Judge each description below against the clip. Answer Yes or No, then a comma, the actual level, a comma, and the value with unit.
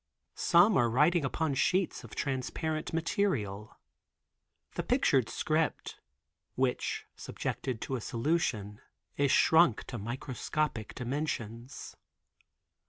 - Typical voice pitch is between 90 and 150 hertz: Yes, low, 135 Hz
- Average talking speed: No, slow, 100 wpm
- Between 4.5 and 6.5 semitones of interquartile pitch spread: Yes, average, 5.3 semitones